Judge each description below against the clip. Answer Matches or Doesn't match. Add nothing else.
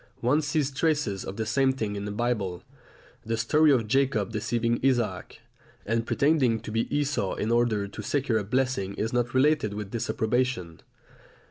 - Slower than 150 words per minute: Doesn't match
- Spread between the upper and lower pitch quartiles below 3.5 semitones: Doesn't match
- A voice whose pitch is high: Doesn't match